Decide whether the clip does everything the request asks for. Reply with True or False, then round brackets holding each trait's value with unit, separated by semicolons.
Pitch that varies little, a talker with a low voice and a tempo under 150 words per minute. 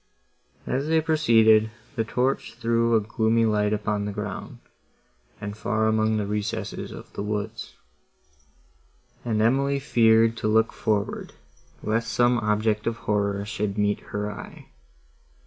True (1.8 semitones; 110 Hz; 135 wpm)